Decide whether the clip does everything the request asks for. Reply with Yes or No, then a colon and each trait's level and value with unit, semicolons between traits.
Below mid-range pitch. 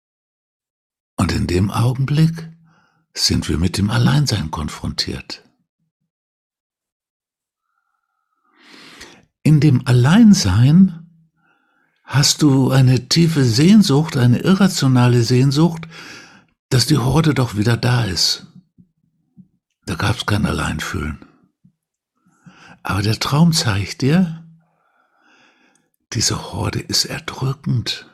No: medium, 145 Hz